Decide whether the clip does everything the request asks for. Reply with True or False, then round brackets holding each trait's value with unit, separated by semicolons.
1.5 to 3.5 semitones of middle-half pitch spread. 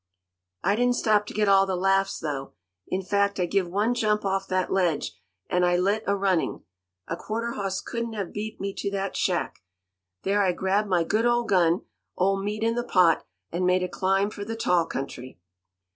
True (2.5 semitones)